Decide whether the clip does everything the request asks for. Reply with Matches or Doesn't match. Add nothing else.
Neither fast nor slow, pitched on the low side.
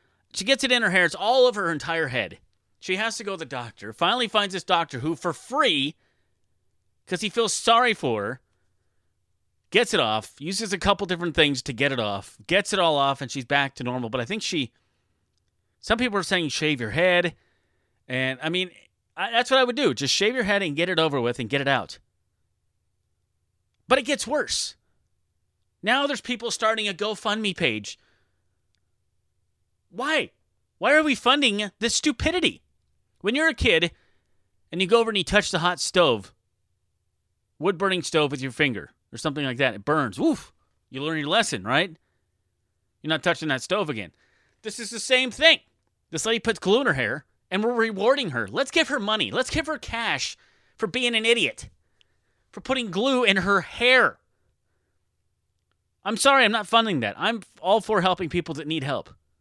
Doesn't match